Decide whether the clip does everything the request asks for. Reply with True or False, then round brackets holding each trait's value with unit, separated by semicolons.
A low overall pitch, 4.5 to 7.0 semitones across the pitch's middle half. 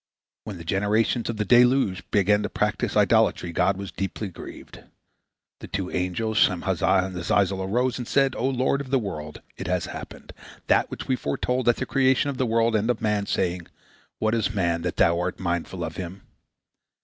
True (100 Hz; 4.8 semitones)